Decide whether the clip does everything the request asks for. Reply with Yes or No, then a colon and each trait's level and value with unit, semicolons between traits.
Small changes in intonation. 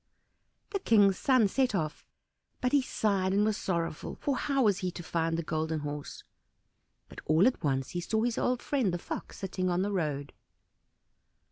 No: wide, 5.6 semitones